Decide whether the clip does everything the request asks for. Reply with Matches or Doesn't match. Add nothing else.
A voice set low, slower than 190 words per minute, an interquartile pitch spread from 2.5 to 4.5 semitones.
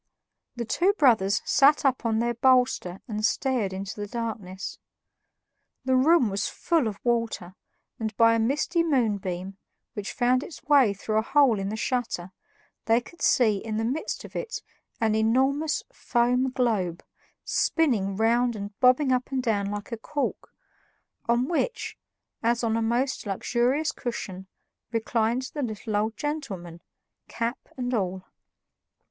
Doesn't match